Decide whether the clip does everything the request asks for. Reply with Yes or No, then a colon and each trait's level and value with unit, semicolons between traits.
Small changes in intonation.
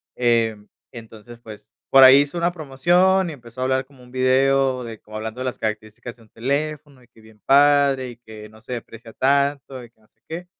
No: average, 3.7 semitones